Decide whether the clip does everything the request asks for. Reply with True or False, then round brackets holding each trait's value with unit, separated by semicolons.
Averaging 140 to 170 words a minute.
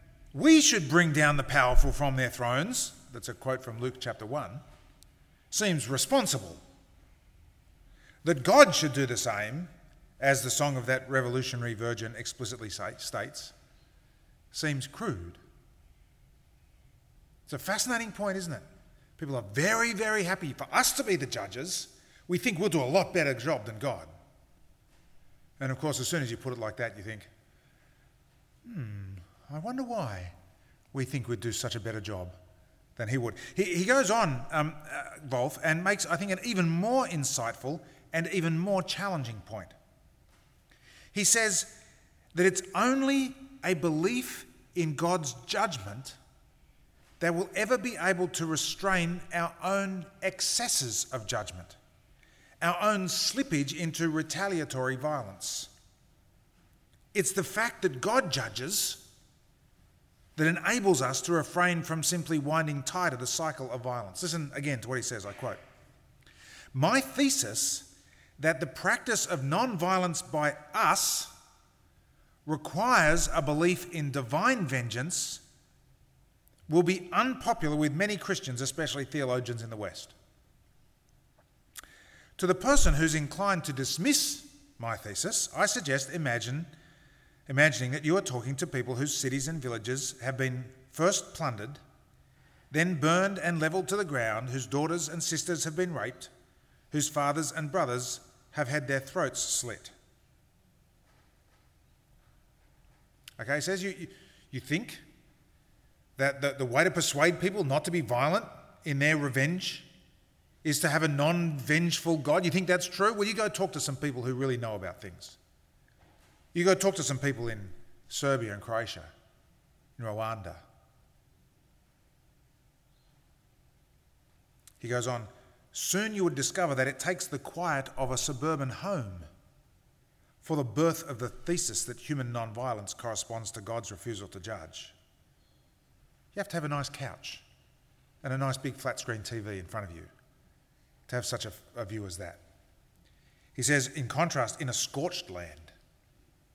True (150 wpm)